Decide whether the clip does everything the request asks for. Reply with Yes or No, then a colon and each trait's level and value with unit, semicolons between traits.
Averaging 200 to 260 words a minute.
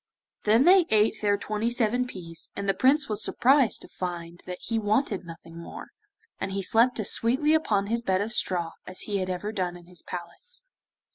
Yes: fast, 205 wpm